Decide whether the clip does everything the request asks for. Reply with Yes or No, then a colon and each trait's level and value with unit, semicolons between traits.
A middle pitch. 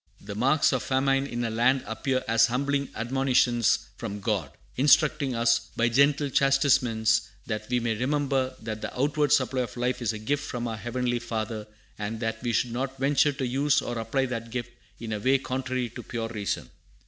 No: low, 125 Hz